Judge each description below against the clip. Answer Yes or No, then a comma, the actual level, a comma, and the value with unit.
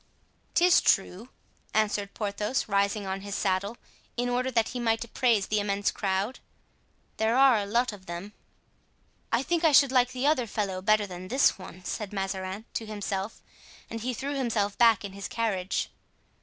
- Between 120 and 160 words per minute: No, average, 170 wpm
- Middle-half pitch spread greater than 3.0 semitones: Yes, average, 3.6 semitones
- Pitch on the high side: Yes, high, 215 Hz